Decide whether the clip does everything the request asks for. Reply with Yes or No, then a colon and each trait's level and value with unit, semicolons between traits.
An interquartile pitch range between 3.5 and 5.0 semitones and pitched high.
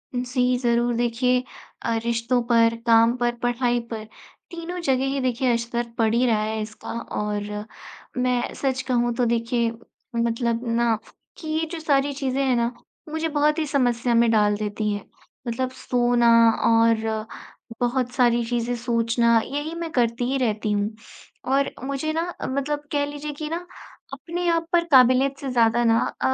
No: average, 2.8 semitones; high, 245 Hz